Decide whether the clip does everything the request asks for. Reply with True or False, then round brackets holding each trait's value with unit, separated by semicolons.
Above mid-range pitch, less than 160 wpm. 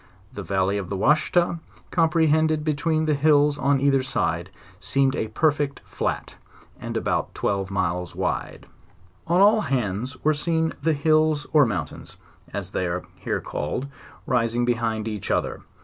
False (140 Hz; 150 wpm)